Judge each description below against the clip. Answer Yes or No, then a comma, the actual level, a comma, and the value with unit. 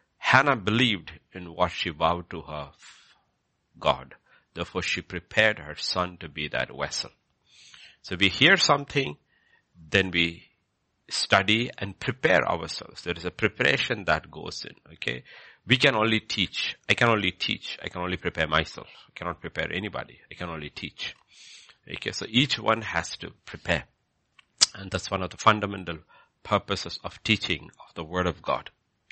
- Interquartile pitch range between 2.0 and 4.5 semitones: Yes, average, 4.2 semitones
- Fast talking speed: No, average, 165 wpm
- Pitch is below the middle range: Yes, very low, 90 Hz